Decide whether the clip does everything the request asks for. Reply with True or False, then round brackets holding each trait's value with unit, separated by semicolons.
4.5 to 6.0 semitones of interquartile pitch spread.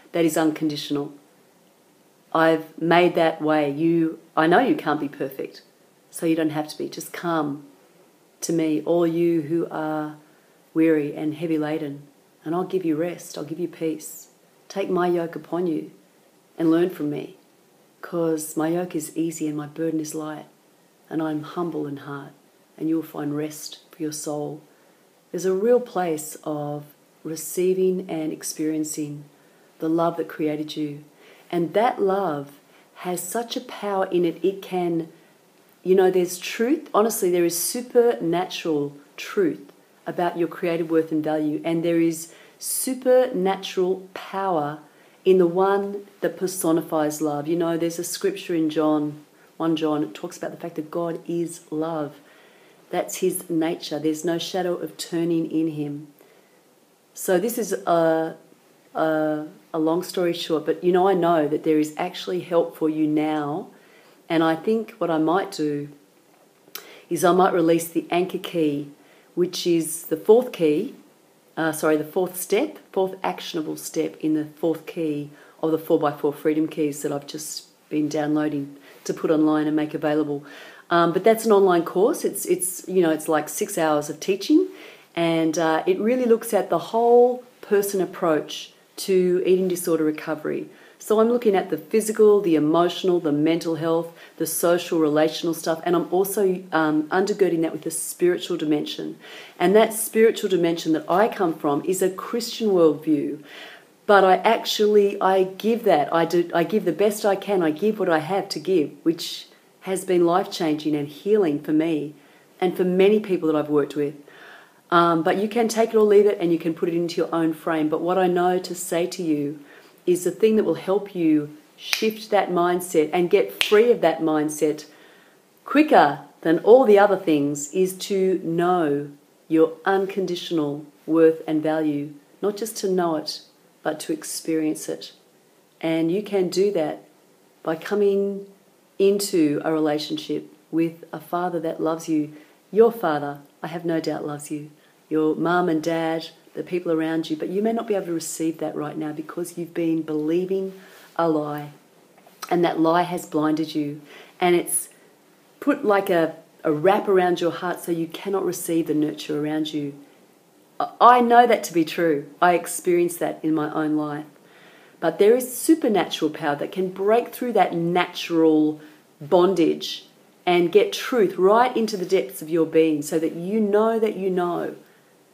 False (3.2 semitones)